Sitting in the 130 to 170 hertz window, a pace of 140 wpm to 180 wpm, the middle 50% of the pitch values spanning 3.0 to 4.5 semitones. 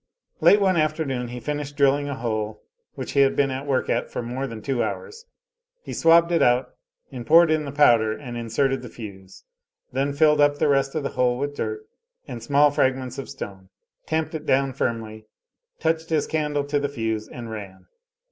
No: low, 135 Hz; average, 195 wpm; average, 3.7 semitones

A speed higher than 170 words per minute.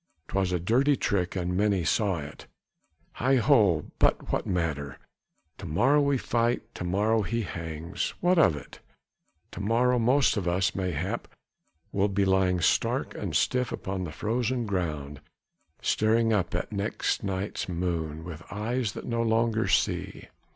No: average, 150 wpm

